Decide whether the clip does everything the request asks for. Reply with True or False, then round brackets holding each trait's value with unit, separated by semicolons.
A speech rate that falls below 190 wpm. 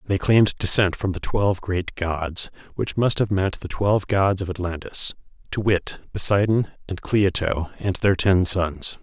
True (175 wpm)